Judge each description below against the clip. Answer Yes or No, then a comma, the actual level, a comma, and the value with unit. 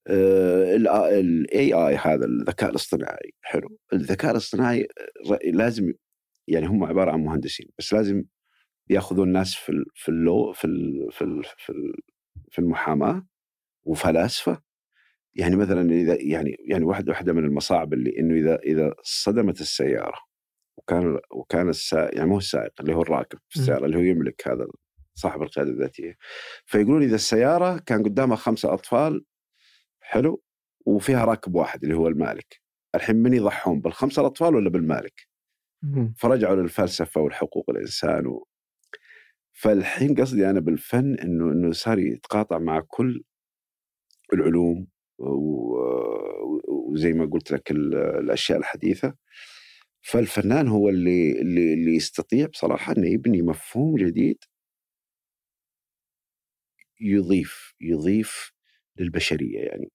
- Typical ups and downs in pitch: No, wide, 6.3 semitones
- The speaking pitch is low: Yes, very low, 95 Hz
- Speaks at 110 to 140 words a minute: Yes, average, 115 wpm